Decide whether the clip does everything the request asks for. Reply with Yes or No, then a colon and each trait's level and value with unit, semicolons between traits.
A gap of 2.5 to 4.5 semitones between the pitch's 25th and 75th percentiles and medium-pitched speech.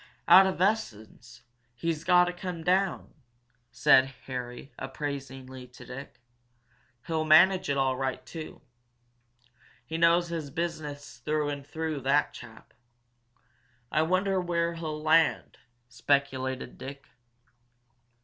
Yes: average, 4.2 semitones; medium, 150 Hz